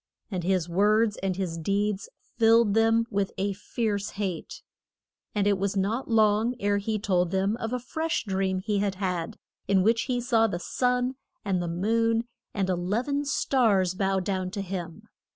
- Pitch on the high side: Yes, high, 200 Hz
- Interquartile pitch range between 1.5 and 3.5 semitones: Yes, average, 3.1 semitones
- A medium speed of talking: Yes, average, 175 wpm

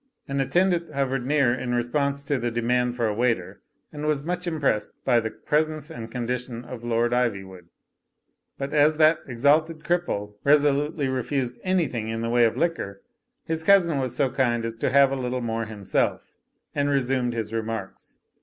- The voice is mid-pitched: No, low, 130 Hz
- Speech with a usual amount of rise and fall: Yes, average, 4.1 semitones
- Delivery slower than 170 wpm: No, average, 175 wpm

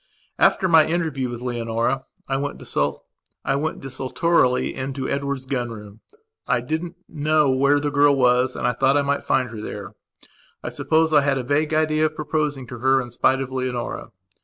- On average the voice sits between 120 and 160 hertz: Yes, low, 135 Hz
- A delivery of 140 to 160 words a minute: No, average, 175 wpm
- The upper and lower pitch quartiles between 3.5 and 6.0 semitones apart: No, average, 3.1 semitones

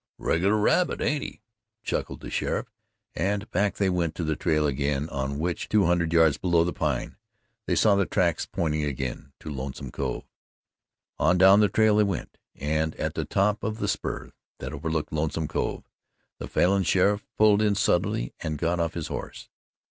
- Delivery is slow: No, average, 180 wpm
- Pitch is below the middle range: Yes, very low, 85 Hz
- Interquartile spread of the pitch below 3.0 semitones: No, average, 4.5 semitones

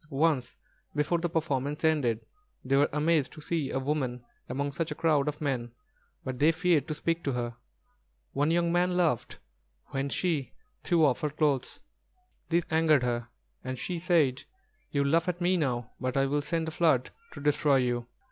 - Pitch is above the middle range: No, medium, 145 Hz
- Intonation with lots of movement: No, average, 3.7 semitones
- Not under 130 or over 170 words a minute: No, average, 180 wpm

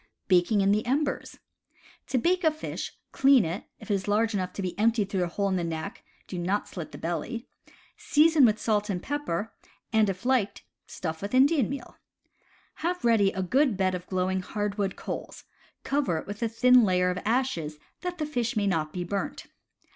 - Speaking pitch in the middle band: No, high, 205 Hz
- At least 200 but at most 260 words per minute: Yes, fast, 205 wpm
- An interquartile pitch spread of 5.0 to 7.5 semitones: Yes, wide, 5.5 semitones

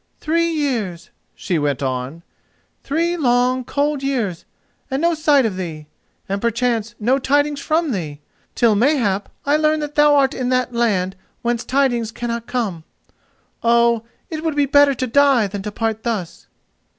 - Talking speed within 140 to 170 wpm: Yes, average, 155 wpm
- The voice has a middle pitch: No, high, 245 Hz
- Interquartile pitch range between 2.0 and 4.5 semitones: No, wide, 5.5 semitones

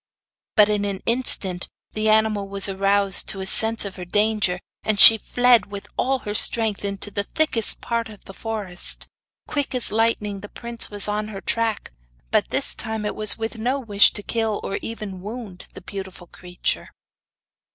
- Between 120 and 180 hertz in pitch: No, high, 210 Hz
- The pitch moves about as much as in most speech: No, narrow, 2.2 semitones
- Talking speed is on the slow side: No, average, 180 wpm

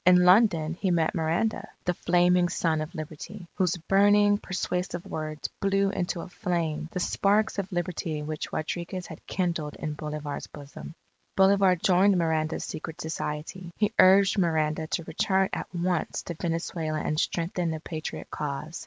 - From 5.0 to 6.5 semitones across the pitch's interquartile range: No, average, 2.9 semitones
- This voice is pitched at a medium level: Yes, medium, 175 Hz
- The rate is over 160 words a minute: No, average, 155 wpm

